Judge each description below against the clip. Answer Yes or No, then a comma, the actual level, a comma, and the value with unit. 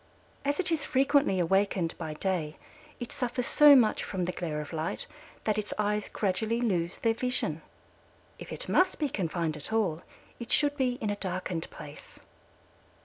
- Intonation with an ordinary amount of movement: No, wide, 6.2 semitones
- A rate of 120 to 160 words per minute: No, average, 170 wpm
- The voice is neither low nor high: No, high, 210 Hz